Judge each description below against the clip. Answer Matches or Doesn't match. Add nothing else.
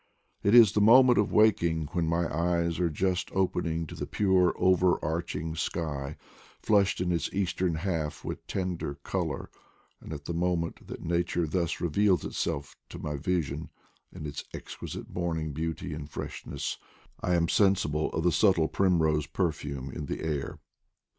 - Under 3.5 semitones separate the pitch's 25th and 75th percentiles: Matches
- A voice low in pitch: Matches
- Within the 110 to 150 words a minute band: Doesn't match